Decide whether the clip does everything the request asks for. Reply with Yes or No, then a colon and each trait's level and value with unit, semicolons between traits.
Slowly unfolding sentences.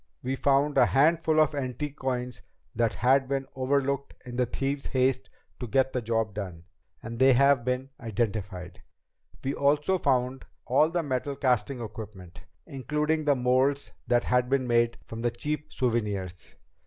No: average, 155 wpm